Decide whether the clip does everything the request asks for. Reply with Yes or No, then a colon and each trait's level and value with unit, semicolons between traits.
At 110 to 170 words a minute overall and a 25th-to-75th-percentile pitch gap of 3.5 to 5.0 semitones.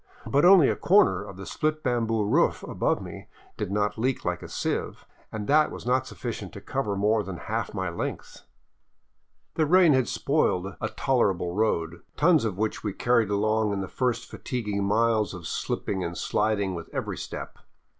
No: average, 180 wpm; average, 4.4 semitones